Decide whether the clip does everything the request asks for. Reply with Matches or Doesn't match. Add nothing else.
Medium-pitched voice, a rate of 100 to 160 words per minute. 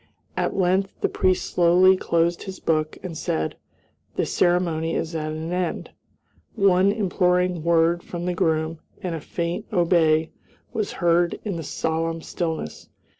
Matches